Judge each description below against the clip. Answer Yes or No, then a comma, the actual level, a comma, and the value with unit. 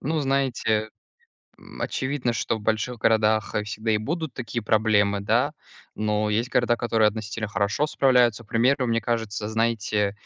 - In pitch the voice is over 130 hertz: No, low, 110 Hz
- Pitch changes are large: No, narrow, 2.5 semitones